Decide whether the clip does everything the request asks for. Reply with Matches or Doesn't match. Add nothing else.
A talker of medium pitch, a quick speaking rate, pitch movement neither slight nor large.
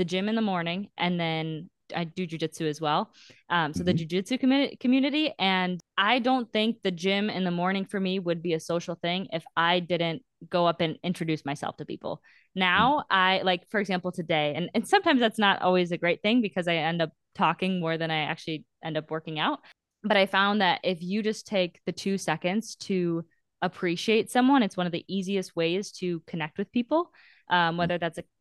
Matches